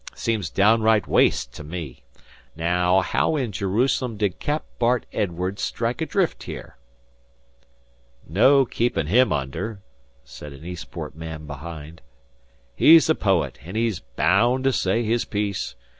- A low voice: Yes, low, 100 Hz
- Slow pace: Yes, slow, 130 wpm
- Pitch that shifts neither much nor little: No, wide, 6.3 semitones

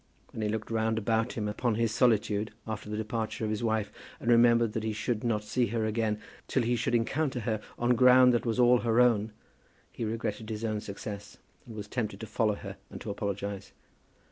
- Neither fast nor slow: No, fast, 210 wpm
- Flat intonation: Yes, narrow, 1.9 semitones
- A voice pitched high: No, low, 110 Hz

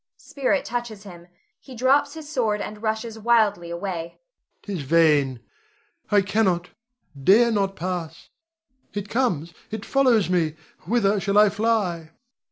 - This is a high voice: Yes, high, 205 Hz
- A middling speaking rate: No, slow, 130 wpm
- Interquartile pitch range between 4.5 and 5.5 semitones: Yes, average, 5.0 semitones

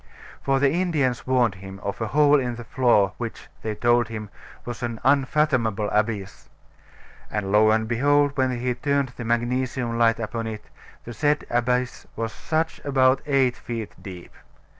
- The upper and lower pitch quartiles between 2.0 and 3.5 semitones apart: Yes, average, 3.2 semitones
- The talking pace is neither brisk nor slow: Yes, average, 160 wpm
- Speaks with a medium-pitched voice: No, low, 120 Hz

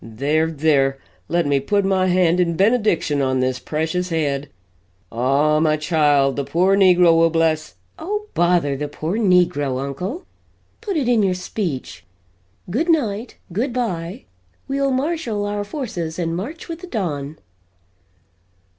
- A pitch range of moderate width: No, wide, 5.9 semitones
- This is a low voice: No, medium, 170 Hz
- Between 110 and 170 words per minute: Yes, average, 145 wpm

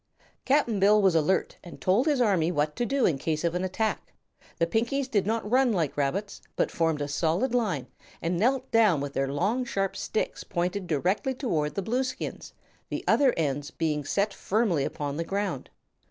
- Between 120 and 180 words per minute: No, average, 190 wpm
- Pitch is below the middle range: No, high, 190 Hz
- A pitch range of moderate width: No, wide, 6.3 semitones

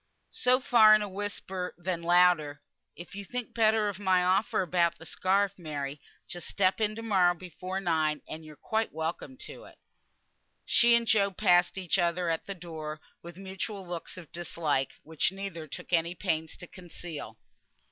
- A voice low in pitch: No, medium, 180 Hz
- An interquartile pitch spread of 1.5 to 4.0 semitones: Yes, average, 3.3 semitones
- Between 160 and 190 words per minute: Yes, average, 175 wpm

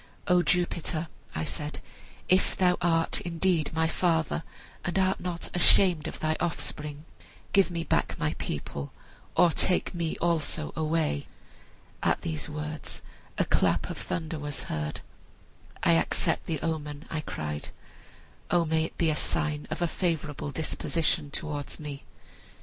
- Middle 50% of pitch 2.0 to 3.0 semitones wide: Yes, narrow, 2.6 semitones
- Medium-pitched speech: Yes, medium, 160 Hz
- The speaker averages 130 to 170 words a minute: Yes, average, 145 wpm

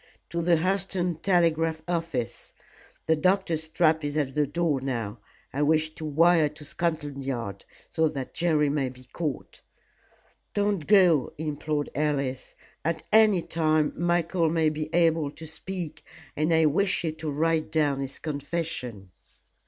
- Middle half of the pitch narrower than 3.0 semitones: Yes, narrow, 2.5 semitones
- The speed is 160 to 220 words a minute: No, average, 145 wpm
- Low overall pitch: No, medium, 155 Hz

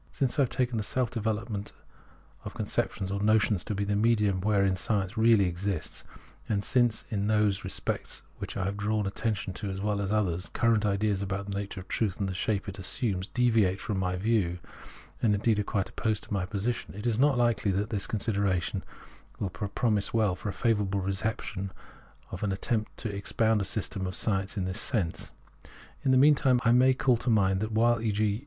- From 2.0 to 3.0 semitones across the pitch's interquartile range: Yes, narrow, 2.5 semitones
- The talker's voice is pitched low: Yes, low, 105 Hz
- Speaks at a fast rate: Yes, fast, 215 wpm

